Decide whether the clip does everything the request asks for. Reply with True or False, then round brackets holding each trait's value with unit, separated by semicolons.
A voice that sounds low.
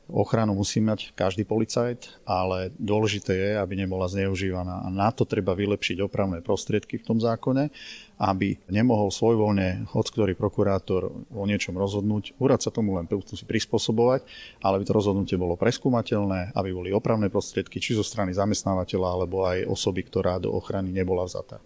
True (100 Hz)